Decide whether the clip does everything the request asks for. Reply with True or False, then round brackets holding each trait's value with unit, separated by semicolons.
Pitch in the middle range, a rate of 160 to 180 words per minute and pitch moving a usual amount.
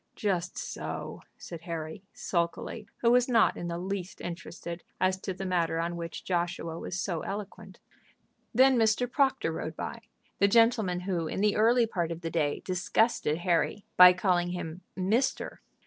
True (180 Hz; 165 wpm; 3.9 semitones)